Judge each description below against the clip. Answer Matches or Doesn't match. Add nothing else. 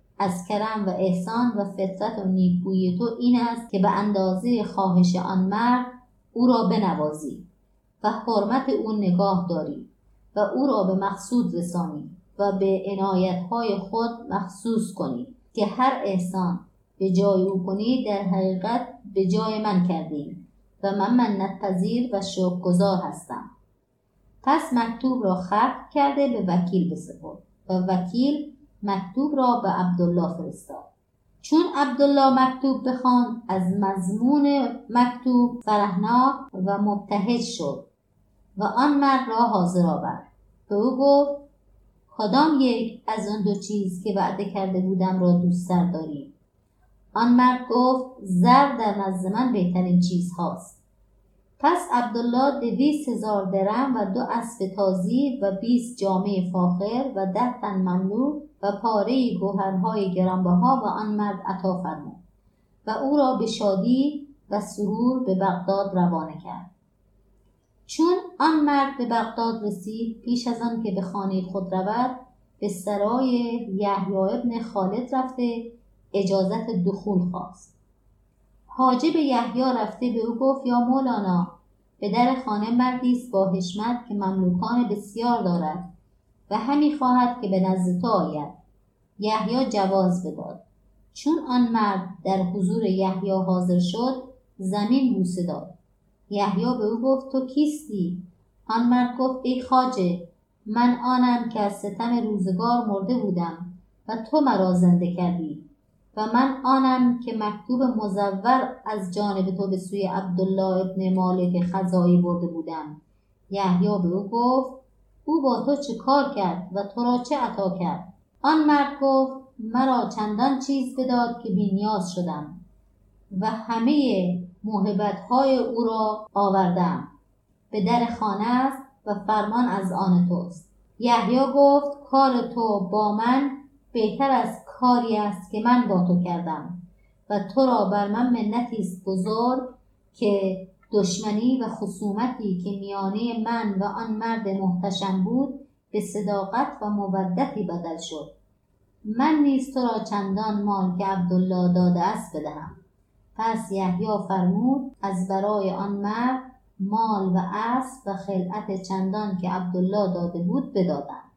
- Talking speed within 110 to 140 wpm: Matches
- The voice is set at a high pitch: Matches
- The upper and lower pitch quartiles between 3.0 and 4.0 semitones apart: Doesn't match